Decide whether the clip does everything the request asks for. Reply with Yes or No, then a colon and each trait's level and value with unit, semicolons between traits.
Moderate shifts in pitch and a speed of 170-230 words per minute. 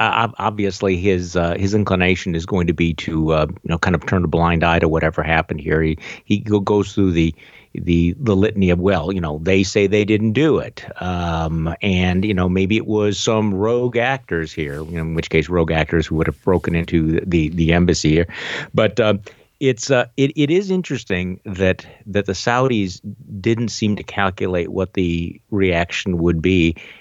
Yes: average, 3.8 semitones; average, 200 wpm